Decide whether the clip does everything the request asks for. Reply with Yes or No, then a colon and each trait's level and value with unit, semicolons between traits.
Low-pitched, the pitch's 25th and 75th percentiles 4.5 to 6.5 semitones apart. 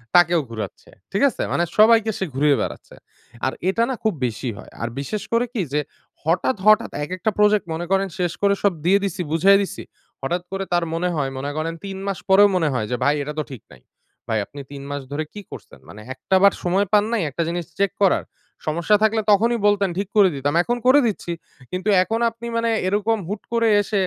No: high, 190 Hz; average, 5.2 semitones